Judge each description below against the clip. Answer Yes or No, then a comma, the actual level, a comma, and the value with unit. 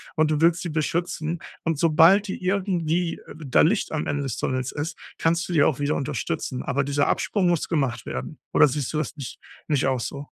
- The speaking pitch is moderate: Yes, medium, 155 Hz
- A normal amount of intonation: Yes, average, 3.0 semitones